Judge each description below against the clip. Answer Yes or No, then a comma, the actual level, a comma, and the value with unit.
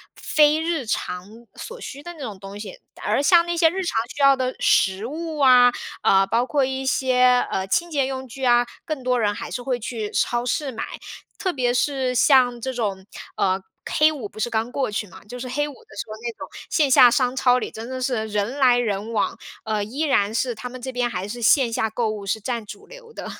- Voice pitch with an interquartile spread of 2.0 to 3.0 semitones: No, average, 3.7 semitones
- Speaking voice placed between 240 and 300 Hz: Yes, very high, 250 Hz